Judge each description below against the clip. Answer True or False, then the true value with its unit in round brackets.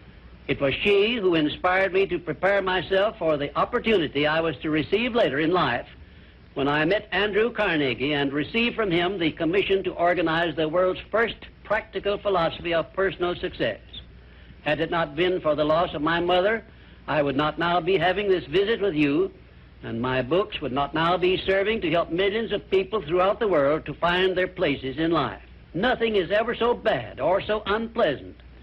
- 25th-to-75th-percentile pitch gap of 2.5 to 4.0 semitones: False (4.8 semitones)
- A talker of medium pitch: True (180 Hz)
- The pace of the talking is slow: False (190 wpm)